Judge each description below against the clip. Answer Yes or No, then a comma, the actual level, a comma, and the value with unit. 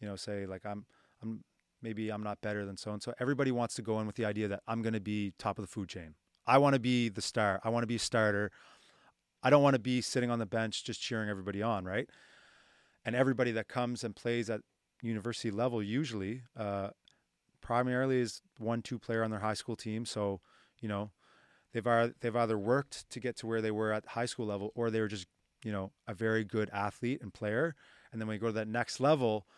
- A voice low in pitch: Yes, low, 110 Hz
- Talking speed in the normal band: No, fast, 240 wpm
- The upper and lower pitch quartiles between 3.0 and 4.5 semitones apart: No, narrow, 2.4 semitones